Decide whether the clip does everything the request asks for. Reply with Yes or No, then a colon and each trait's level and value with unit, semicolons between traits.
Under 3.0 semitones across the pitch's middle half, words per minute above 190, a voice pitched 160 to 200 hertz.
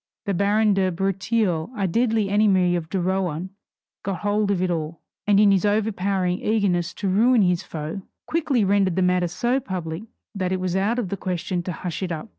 Yes: narrow, 2.5 semitones; average, 200 wpm; high, 190 Hz